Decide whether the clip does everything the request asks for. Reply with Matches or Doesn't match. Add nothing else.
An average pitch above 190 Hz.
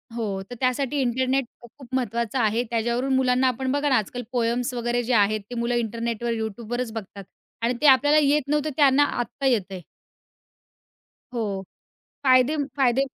Matches